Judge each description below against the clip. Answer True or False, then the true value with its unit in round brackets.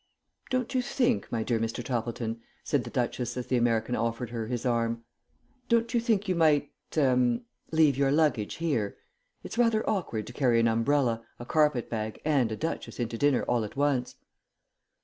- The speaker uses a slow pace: False (180 wpm)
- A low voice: True (125 Hz)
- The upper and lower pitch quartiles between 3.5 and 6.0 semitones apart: True (5.0 semitones)